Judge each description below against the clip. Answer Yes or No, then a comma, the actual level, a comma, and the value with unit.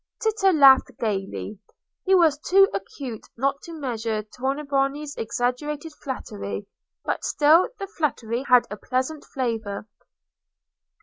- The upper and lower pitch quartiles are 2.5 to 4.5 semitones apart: No, average, 5.0 semitones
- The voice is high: Yes, very high, 270 Hz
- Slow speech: Yes, slow, 115 wpm